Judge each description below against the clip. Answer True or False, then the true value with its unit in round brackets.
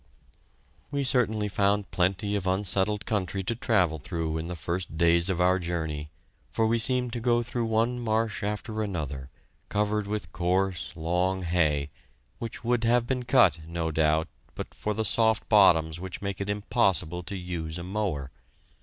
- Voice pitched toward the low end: True (95 Hz)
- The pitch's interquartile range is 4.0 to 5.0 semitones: True (4.5 semitones)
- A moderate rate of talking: True (165 wpm)